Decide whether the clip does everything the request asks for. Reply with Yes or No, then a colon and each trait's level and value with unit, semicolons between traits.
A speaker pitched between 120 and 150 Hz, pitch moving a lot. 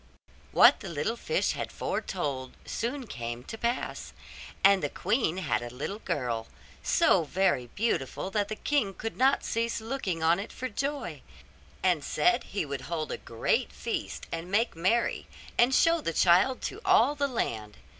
No: high, 195 Hz; wide, 7.8 semitones